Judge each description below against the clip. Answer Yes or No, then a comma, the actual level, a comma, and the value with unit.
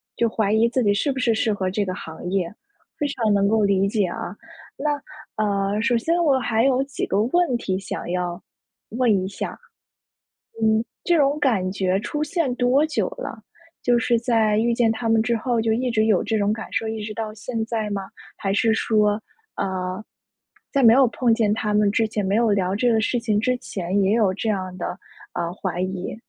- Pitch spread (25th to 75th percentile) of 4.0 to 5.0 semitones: No, average, 3.3 semitones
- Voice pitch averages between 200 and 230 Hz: Yes, high, 220 Hz